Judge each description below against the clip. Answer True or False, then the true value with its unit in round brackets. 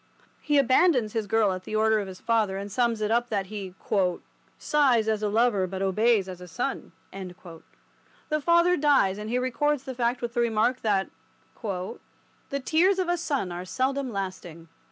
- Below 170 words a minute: False (180 wpm)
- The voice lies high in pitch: True (220 Hz)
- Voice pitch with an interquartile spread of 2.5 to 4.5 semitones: False (5.1 semitones)